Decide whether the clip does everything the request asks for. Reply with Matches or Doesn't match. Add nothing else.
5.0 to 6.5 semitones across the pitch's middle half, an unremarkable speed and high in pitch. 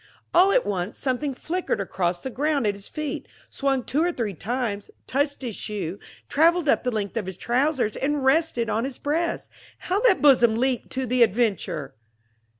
Matches